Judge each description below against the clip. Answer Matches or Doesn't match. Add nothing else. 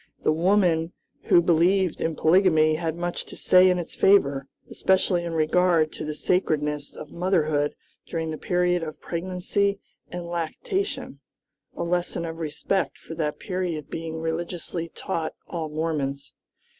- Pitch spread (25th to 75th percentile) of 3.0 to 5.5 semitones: Doesn't match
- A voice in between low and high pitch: Matches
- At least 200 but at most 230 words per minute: Doesn't match